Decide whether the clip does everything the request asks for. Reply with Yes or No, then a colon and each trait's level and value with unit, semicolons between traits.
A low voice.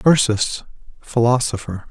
Yes: low, 115 Hz